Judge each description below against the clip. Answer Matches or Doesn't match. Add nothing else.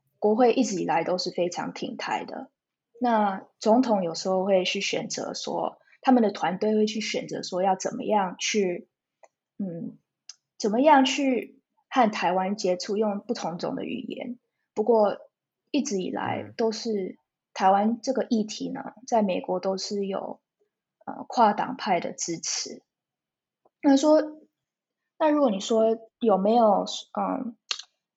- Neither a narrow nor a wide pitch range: Matches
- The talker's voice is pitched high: Matches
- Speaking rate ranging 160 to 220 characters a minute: Matches